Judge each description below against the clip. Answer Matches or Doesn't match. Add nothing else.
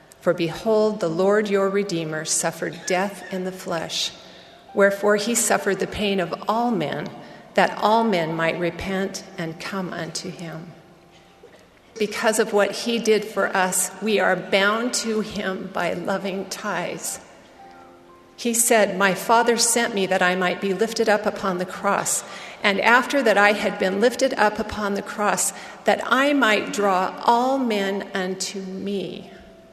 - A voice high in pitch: Matches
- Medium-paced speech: Matches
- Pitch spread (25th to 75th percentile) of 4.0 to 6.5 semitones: Doesn't match